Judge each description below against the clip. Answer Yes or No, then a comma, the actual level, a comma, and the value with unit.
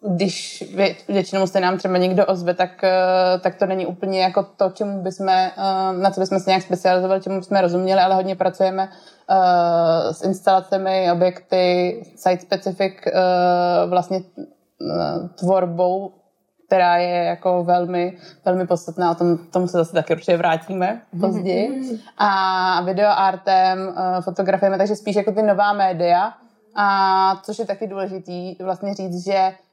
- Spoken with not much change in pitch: Yes, narrow, 1.2 semitones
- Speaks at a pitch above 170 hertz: Yes, high, 190 Hz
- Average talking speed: Yes, average, 135 wpm